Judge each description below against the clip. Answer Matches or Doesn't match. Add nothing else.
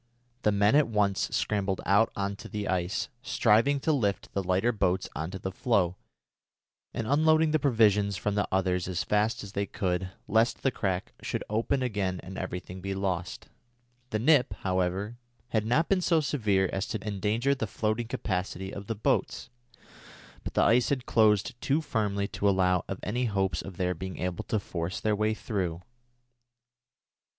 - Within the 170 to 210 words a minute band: Matches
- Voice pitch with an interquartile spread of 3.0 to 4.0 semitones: Matches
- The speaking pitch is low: Matches